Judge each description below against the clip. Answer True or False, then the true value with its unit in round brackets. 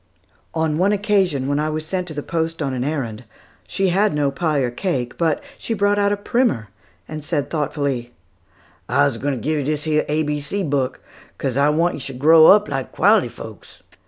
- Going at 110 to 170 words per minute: False (205 wpm)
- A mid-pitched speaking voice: True (150 Hz)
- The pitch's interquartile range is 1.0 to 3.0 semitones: False (4.0 semitones)